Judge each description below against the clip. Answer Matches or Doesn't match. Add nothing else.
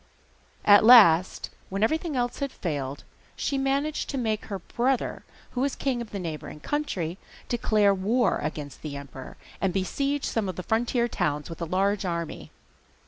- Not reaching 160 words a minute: Doesn't match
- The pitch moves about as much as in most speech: Doesn't match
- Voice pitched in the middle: Doesn't match